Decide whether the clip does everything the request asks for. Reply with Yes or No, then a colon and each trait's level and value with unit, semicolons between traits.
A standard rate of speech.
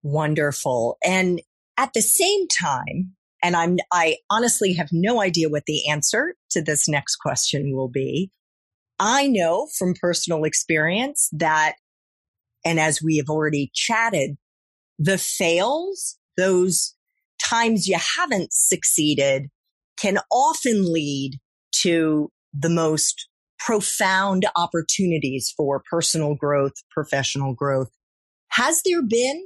No: slow, 115 wpm